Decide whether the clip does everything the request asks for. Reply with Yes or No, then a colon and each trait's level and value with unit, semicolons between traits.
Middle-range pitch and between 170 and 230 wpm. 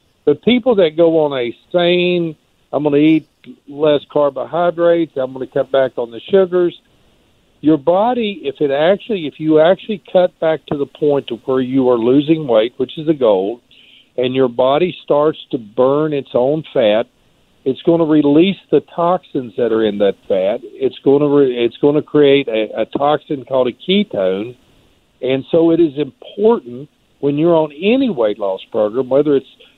Yes: medium, 145 Hz; average, 185 wpm